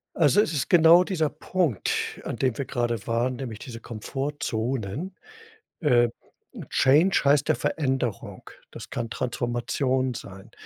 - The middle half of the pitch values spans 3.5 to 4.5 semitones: Yes, average, 4.1 semitones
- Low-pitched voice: Yes, low, 130 Hz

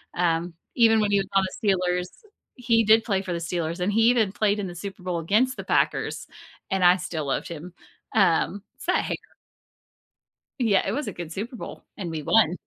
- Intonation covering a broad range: No, average, 3.7 semitones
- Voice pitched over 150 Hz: Yes, high, 190 Hz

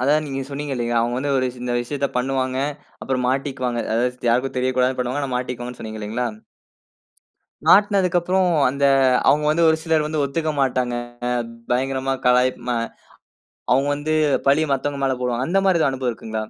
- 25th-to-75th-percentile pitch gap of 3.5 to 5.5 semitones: No, average, 2.7 semitones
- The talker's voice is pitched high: No, low, 130 Hz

